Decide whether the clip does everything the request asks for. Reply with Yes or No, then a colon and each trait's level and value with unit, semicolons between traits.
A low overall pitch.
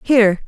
No: high, 220 Hz